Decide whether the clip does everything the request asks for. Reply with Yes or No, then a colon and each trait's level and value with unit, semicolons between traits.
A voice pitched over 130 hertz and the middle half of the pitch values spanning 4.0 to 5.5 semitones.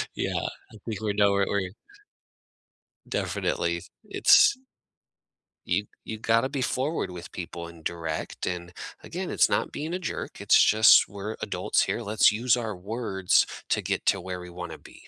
No: low, 100 Hz; average, 4.3 semitones